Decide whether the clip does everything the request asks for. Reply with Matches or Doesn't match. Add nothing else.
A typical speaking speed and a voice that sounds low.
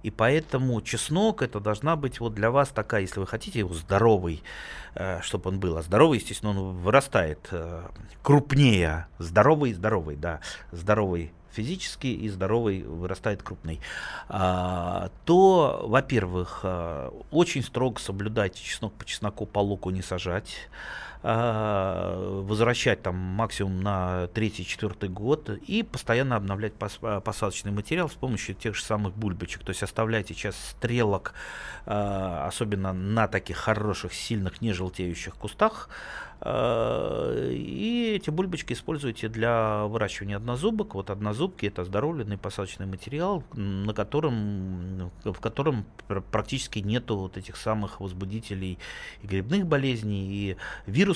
Matches